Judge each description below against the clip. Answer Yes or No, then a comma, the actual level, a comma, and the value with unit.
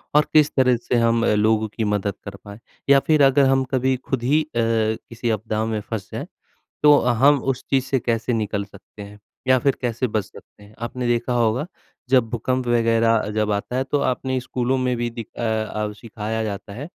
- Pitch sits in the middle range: No, low, 115 Hz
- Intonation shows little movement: No, average, 3.0 semitones